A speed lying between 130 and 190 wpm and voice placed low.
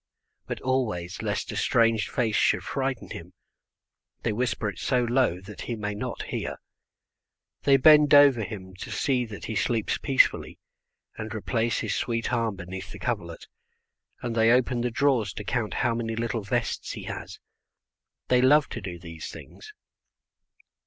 Yes: average, 160 wpm; low, 115 Hz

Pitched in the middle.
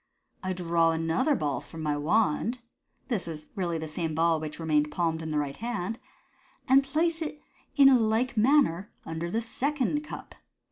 Yes: medium, 175 Hz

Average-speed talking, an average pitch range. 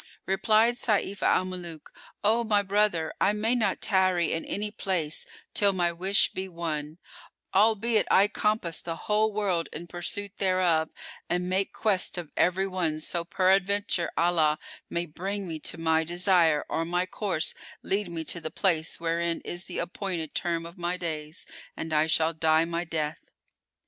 Yes: average, 165 wpm; average, 3.2 semitones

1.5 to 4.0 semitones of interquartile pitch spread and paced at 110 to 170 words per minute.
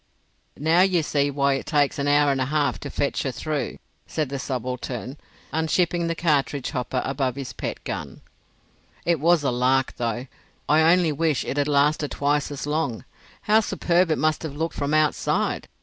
No: average, 2.9 semitones; average, 180 wpm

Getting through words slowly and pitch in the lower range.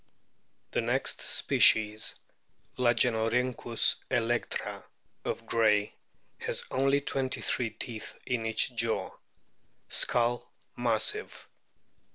Yes: slow, 85 wpm; low, 115 Hz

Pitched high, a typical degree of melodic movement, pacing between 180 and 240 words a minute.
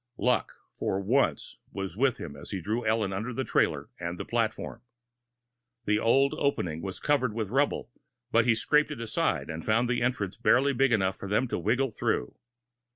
No: low, 115 Hz; average, 4.7 semitones; average, 185 wpm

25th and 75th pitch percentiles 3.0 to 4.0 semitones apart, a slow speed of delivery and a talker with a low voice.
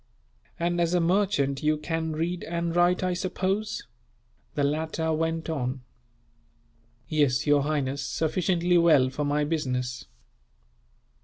No: average, 3.3 semitones; slow, 125 wpm; medium, 160 Hz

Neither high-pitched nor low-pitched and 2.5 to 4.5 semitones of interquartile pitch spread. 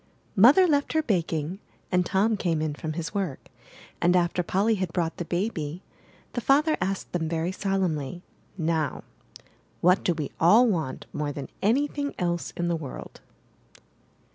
Yes: medium, 180 Hz; average, 4.1 semitones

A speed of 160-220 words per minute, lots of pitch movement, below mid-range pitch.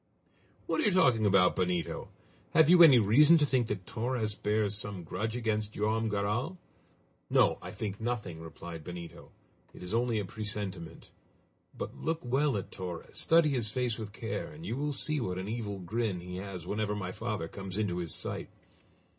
No: average, 180 wpm; average, 4.6 semitones; low, 105 Hz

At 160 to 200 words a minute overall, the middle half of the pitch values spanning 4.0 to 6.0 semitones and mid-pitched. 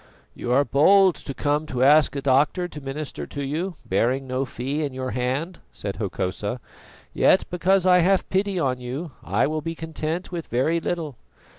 Yes: average, 180 wpm; average, 4.6 semitones; medium, 145 Hz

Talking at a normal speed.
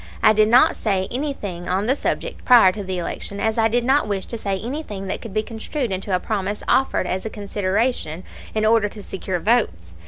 No: fast, 215 wpm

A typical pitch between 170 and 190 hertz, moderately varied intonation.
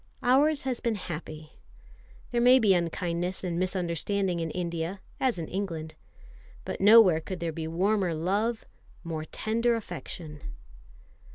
Yes: medium, 185 Hz; average, 4.7 semitones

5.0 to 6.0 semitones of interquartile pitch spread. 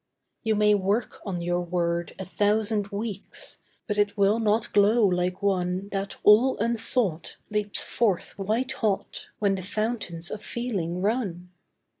No: average, 3.0 semitones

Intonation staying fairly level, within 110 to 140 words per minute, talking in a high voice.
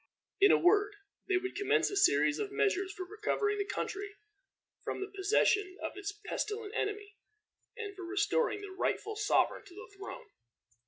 No: narrow, 1.4 semitones; average, 165 wpm; very high, 405 Hz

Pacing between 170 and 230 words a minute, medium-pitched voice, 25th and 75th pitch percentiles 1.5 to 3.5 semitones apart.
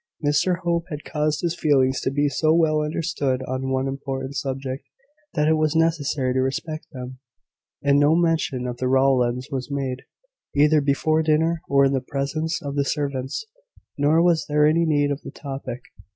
Yes: average, 180 wpm; medium, 145 Hz; average, 2.8 semitones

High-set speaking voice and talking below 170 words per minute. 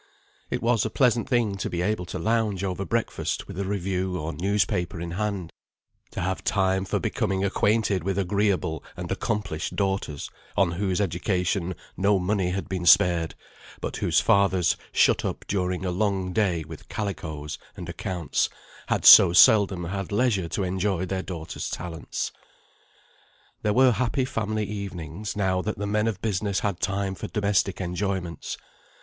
No: very low, 95 Hz; average, 160 wpm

